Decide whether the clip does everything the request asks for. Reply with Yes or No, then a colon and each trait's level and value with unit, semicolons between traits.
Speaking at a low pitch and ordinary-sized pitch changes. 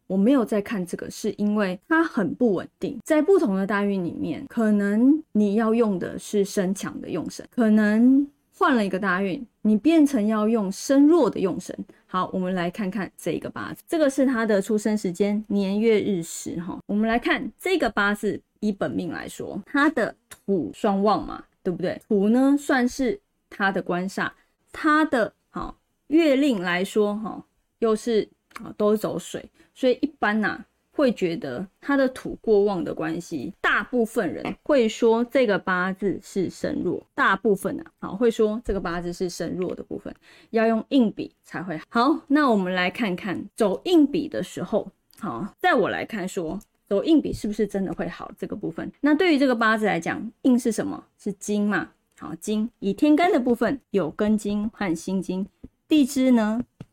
No: high, 215 Hz; average, 5.0 semitones